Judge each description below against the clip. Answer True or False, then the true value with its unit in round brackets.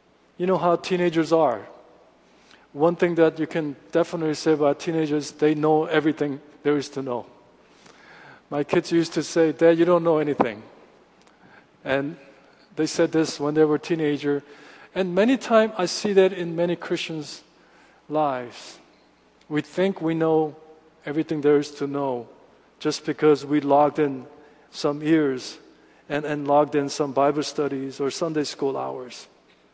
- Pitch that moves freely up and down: False (2.4 semitones)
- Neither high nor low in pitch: True (155 Hz)